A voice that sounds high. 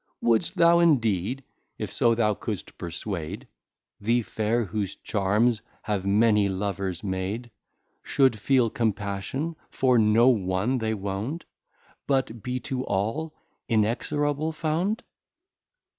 No: low, 110 Hz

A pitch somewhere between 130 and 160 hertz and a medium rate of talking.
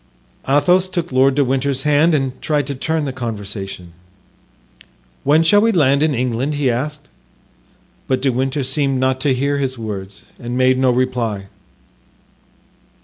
Yes: low, 135 Hz; average, 150 wpm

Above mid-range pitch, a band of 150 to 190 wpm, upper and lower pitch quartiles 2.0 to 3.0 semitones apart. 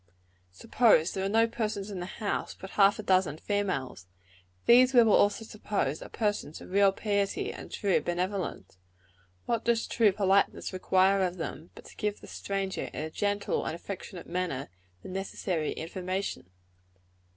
Yes: high, 195 Hz; average, 160 wpm; narrow, 2.5 semitones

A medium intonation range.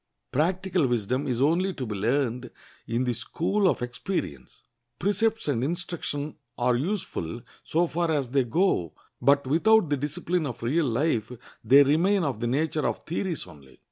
No: wide, 6.1 semitones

